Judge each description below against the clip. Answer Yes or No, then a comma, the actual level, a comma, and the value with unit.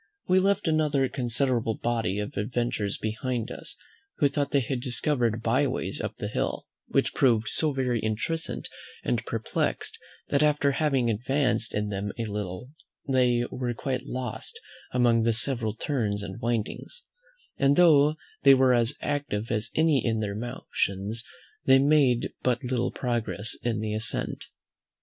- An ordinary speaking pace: Yes, average, 150 wpm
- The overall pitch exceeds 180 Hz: No, low, 120 Hz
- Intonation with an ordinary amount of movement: Yes, average, 3.8 semitones